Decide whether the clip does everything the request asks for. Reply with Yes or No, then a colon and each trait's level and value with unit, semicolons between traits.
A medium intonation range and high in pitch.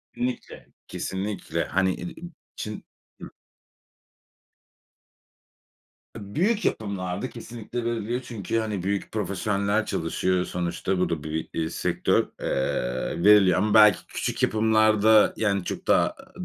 No: average, 3.0 semitones; low, 105 Hz